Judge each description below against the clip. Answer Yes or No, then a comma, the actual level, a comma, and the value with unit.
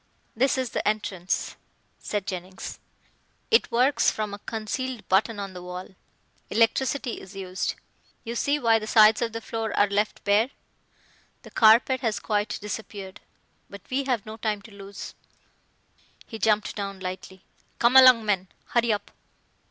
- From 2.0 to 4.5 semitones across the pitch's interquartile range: Yes, average, 2.8 semitones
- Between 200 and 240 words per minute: No, average, 150 wpm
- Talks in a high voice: Yes, high, 215 Hz